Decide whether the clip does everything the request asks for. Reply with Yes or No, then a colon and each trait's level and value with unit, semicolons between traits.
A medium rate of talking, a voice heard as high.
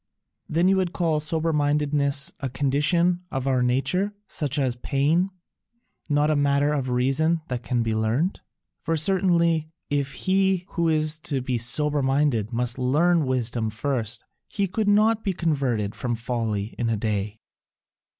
No: average, 155 wpm; medium, 145 Hz